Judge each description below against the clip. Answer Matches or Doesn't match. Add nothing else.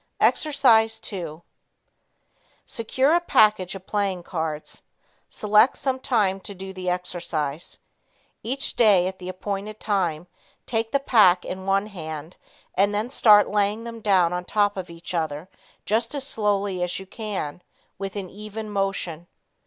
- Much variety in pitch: Doesn't match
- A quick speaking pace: Doesn't match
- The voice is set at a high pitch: Matches